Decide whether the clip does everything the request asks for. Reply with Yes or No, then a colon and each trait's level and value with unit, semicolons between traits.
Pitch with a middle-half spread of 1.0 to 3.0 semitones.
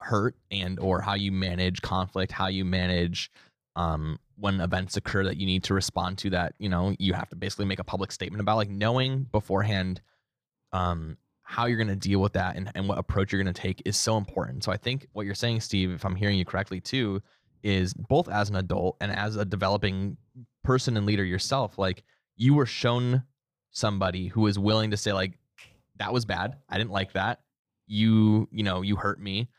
Yes: narrow, 2.6 semitones